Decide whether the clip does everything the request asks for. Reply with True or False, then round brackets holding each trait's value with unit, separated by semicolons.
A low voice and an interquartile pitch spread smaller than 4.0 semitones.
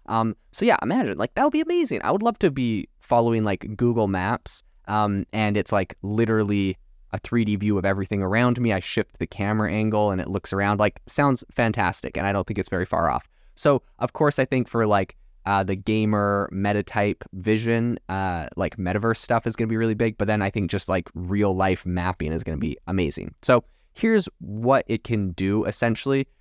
True (105 Hz; 3.3 semitones)